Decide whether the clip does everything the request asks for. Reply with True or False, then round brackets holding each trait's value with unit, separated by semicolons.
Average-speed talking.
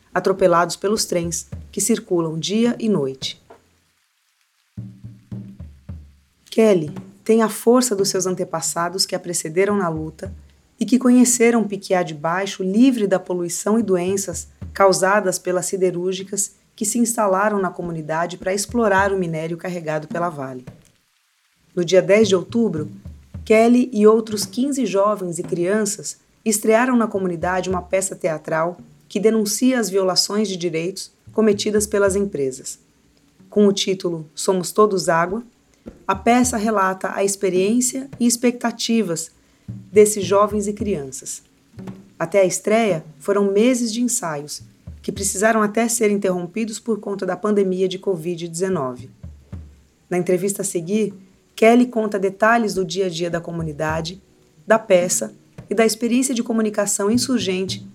True (135 wpm)